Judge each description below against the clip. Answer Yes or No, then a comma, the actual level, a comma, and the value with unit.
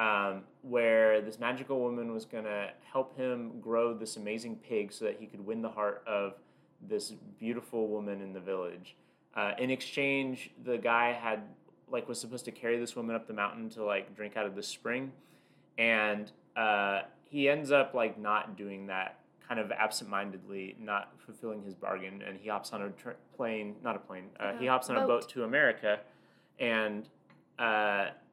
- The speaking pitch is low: Yes, low, 110 Hz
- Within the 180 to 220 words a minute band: Yes, average, 185 wpm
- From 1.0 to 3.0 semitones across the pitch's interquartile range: Yes, average, 2.7 semitones